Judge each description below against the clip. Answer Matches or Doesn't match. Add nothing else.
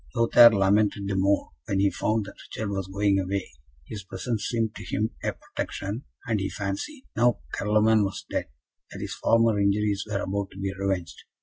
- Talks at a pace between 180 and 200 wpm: Matches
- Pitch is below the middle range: Matches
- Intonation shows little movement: Matches